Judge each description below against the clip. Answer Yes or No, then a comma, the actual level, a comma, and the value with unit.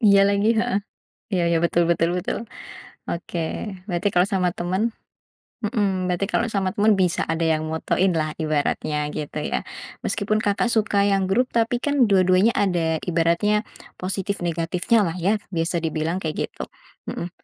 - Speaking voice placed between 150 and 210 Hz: Yes, medium, 185 Hz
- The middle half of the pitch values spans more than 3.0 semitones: Yes, average, 3.5 semitones